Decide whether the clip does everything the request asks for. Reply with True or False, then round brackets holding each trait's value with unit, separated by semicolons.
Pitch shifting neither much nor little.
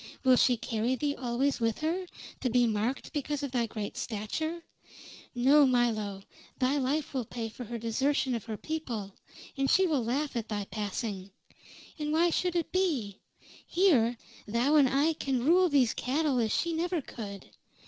True (4.9 semitones)